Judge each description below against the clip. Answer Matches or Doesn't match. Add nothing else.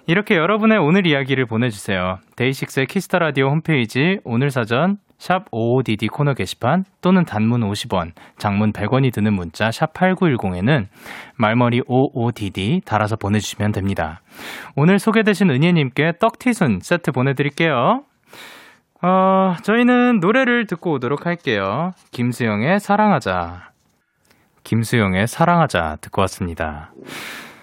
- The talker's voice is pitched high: Doesn't match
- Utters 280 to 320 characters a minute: Matches